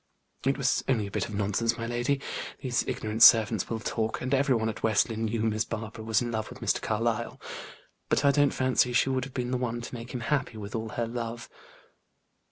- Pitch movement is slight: Yes, narrow, 2.2 semitones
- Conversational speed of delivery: No, fast, 225 wpm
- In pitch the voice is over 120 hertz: No, low, 115 Hz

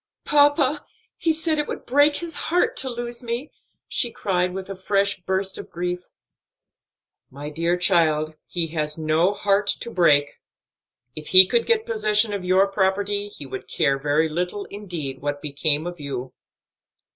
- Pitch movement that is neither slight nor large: No, wide, 6.4 semitones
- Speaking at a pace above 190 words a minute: No, average, 160 wpm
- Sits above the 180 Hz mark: Yes, high, 190 Hz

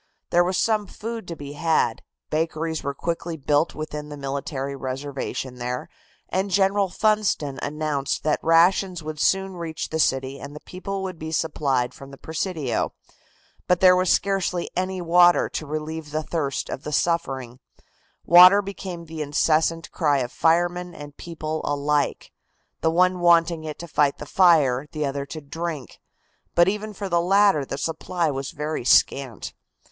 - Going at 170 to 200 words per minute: No, average, 160 wpm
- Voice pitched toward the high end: No, medium, 160 Hz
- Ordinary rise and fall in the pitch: Yes, average, 3.6 semitones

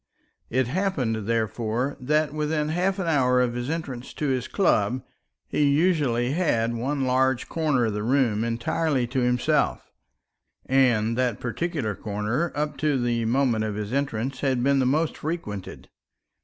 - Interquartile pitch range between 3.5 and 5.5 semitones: Yes, average, 4.3 semitones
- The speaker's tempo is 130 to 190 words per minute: Yes, average, 155 wpm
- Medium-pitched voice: No, low, 130 Hz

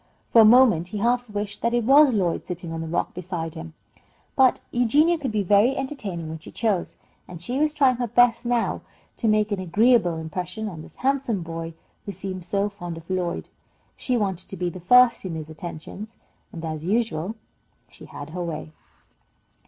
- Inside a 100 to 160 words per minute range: No, average, 190 wpm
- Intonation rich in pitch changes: Yes, wide, 6.0 semitones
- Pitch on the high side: Yes, high, 200 Hz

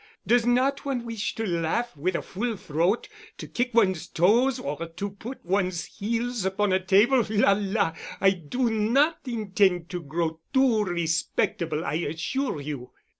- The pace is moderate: Yes, average, 160 wpm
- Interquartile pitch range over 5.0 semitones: Yes, wide, 5.6 semitones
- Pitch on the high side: Yes, high, 200 Hz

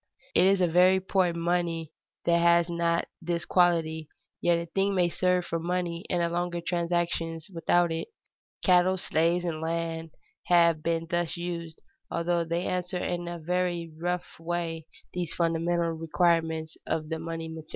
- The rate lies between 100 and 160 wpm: Yes, average, 155 wpm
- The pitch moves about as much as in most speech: No, narrow, 1.2 semitones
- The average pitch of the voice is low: No, medium, 170 Hz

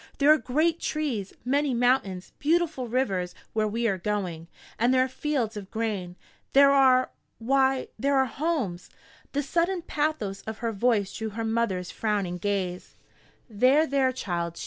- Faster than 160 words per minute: No, average, 155 wpm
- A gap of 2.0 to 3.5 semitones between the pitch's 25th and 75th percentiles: No, wide, 5.6 semitones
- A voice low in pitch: No, high, 235 Hz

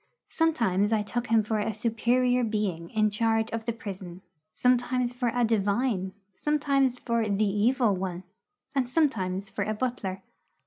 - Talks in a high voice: Yes, high, 225 Hz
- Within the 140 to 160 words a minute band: Yes, average, 150 wpm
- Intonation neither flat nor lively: Yes, average, 3.6 semitones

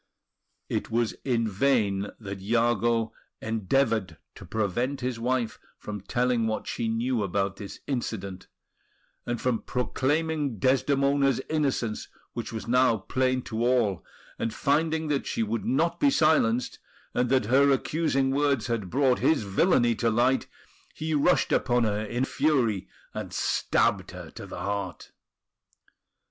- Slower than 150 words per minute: Yes, average, 140 wpm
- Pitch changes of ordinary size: Yes, average, 3.7 semitones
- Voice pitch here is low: Yes, low, 120 Hz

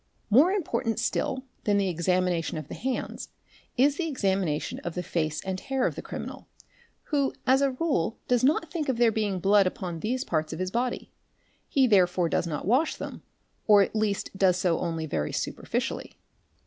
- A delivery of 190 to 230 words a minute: Yes, average, 195 wpm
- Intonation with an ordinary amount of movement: No, wide, 6.5 semitones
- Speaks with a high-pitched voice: Yes, high, 205 Hz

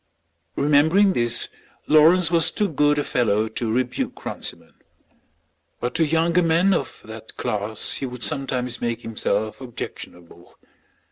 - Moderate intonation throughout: No, wide, 6.1 semitones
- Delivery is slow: Yes, slow, 130 wpm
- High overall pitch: No, low, 130 Hz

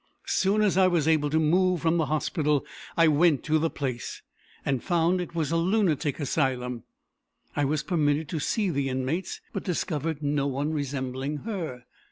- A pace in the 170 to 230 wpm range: Yes, average, 180 wpm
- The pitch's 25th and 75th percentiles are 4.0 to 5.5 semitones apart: No, average, 3.4 semitones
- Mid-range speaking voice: Yes, medium, 155 Hz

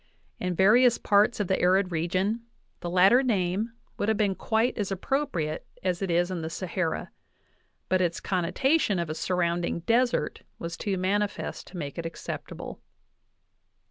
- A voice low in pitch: No, medium, 185 Hz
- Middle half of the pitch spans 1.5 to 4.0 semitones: Yes, average, 3.5 semitones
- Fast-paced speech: No, average, 155 wpm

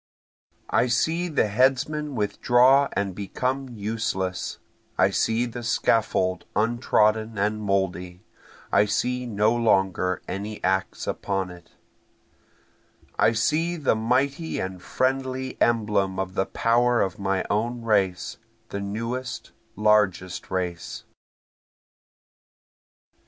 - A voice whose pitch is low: Yes, low, 110 Hz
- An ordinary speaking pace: No, slow, 105 wpm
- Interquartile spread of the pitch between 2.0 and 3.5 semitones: No, average, 4.4 semitones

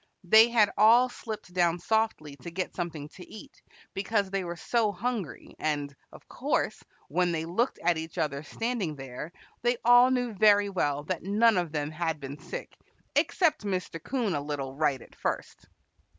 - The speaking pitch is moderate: Yes, medium, 180 Hz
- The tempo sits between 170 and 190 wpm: Yes, average, 175 wpm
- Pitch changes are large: Yes, wide, 6.2 semitones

